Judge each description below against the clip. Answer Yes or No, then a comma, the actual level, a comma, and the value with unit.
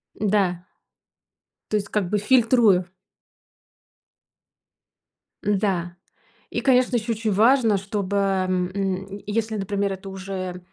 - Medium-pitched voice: No, high, 200 Hz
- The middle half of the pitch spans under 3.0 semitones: Yes, narrow, 2.4 semitones